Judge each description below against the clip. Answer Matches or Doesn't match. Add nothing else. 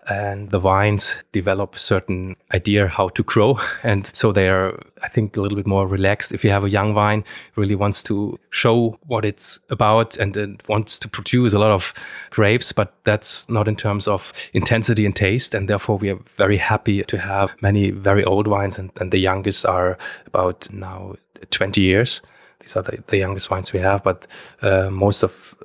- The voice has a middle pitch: Doesn't match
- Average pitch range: Doesn't match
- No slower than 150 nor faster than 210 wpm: Matches